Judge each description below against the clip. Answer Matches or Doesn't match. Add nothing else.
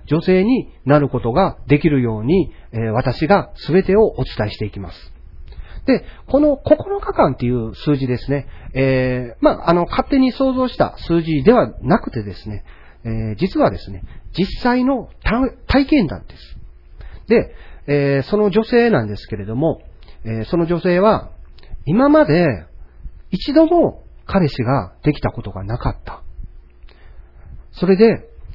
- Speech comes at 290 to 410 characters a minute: Doesn't match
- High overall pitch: Doesn't match